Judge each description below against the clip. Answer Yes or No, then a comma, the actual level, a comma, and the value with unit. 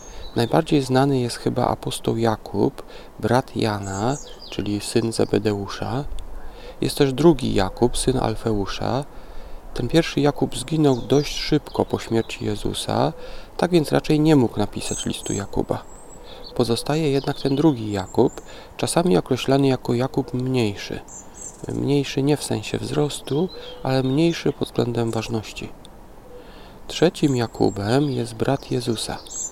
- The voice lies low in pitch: Yes, low, 125 Hz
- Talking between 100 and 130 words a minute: Yes, average, 120 wpm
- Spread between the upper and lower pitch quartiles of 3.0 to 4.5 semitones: Yes, average, 3.8 semitones